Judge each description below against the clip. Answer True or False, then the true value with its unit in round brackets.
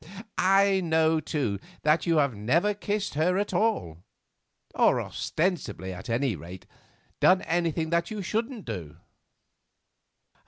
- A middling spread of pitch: False (8.9 semitones)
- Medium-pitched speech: True (160 Hz)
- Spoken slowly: True (125 wpm)